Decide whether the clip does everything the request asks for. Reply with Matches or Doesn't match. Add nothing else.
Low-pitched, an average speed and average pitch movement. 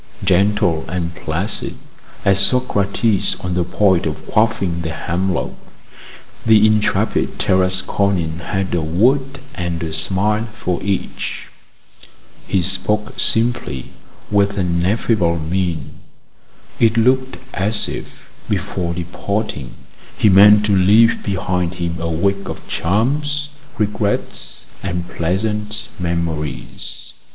Doesn't match